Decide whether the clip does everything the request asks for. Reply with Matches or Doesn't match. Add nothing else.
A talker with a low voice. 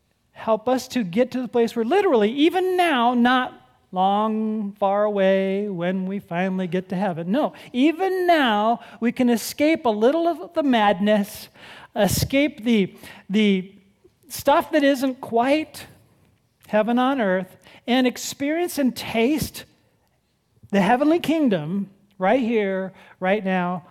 Doesn't match